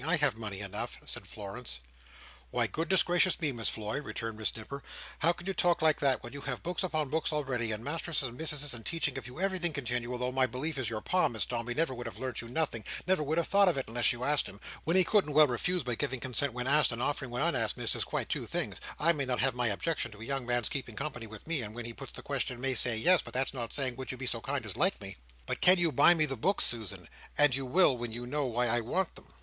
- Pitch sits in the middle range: No, low, 130 Hz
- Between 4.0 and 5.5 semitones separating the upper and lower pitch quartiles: Yes, average, 4.5 semitones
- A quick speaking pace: Yes, fast, 275 wpm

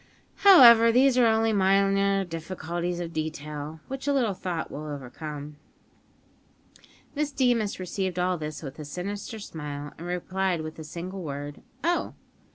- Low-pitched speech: No, medium, 180 Hz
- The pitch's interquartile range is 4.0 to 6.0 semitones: Yes, wide, 5.4 semitones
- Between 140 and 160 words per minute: Yes, average, 145 wpm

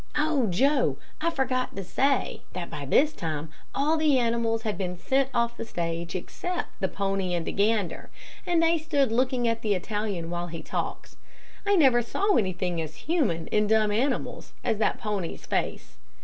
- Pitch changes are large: Yes, wide, 7.0 semitones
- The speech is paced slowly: No, average, 175 wpm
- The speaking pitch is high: Yes, high, 220 Hz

